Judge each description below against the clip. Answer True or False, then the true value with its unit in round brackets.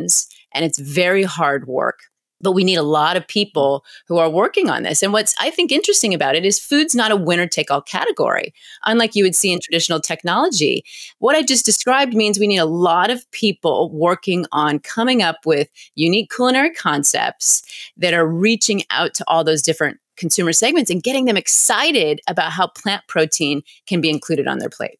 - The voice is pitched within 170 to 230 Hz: True (185 Hz)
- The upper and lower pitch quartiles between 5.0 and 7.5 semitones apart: True (5.5 semitones)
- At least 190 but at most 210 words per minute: True (195 wpm)